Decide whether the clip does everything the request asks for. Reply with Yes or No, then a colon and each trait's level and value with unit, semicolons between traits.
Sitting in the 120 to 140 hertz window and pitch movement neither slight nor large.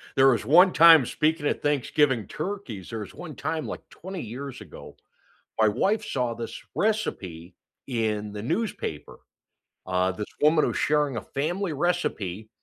No: low, 135 Hz; wide, 7.1 semitones